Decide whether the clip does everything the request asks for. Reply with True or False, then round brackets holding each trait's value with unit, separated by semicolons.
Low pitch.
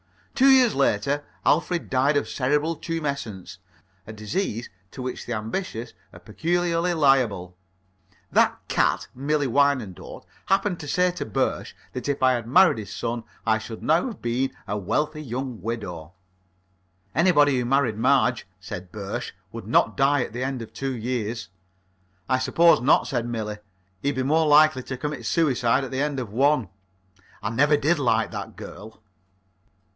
True (130 Hz)